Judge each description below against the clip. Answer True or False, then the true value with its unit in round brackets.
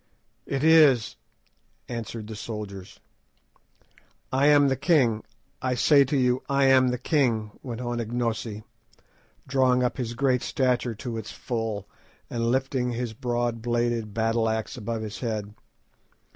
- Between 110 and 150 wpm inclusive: True (140 wpm)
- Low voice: True (120 Hz)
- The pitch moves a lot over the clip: False (2.6 semitones)